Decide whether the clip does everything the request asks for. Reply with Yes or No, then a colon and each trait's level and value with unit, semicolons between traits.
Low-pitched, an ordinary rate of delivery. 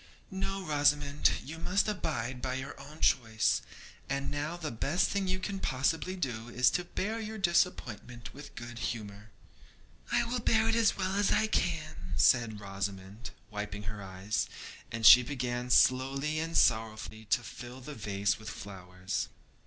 Yes: low, 130 Hz; average, 160 wpm